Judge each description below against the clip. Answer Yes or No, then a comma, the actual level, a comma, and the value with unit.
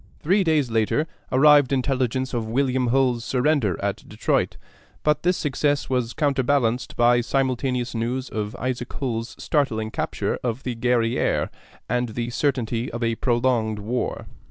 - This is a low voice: Yes, low, 125 Hz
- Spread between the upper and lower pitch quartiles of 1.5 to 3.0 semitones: Yes, average, 2.7 semitones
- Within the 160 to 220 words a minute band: No, average, 140 wpm